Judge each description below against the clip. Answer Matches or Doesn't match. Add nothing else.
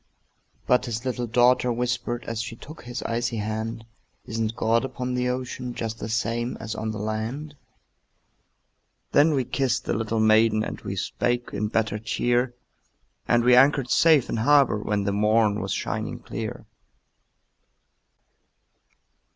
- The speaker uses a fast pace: Doesn't match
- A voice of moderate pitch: Doesn't match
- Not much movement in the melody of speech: Matches